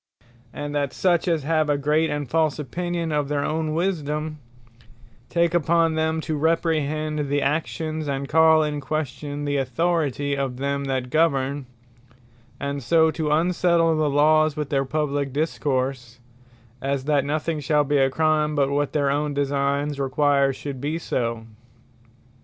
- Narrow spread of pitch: Yes, narrow, 2.2 semitones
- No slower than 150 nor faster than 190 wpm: Yes, average, 155 wpm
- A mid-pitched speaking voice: Yes, medium, 150 Hz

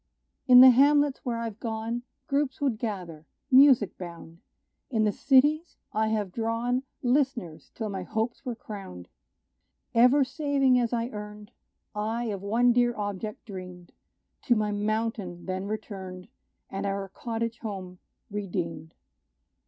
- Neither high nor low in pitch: No, high, 220 Hz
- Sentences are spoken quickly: No, slow, 135 wpm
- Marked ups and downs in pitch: No, average, 4.0 semitones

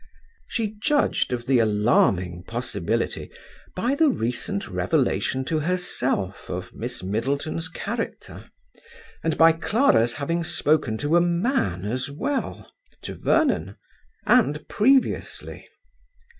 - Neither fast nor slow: No, slow, 110 wpm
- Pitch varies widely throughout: Yes, wide, 7.7 semitones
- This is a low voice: No, medium, 150 Hz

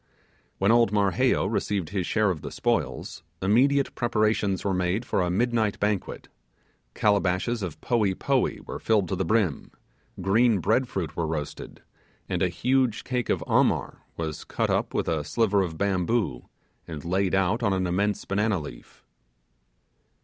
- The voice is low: Yes, low, 100 Hz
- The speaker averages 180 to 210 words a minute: No, average, 155 wpm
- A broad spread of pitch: No, average, 3.8 semitones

